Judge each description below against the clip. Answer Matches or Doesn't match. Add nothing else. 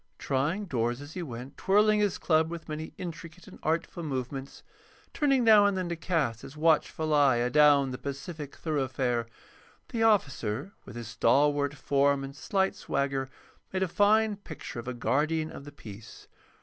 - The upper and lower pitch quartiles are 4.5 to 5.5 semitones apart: Matches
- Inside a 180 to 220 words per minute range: Doesn't match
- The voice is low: Doesn't match